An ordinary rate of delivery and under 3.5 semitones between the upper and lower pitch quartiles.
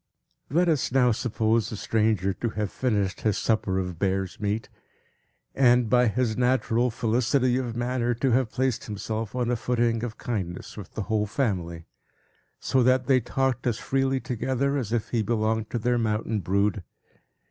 Yes: average, 170 wpm; average, 2.9 semitones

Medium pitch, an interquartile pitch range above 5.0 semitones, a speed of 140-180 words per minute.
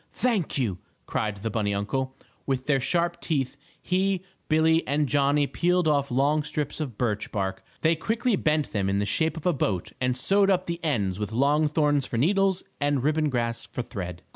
No: medium, 145 Hz; wide, 5.6 semitones; average, 190 wpm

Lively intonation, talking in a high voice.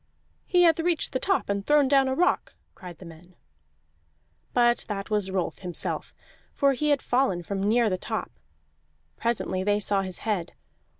Yes: wide, 6.4 semitones; high, 210 Hz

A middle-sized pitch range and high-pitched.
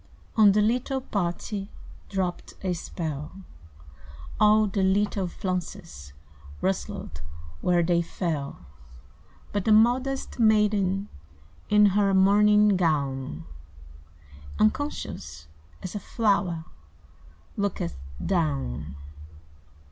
Yes: average, 4.3 semitones; high, 195 Hz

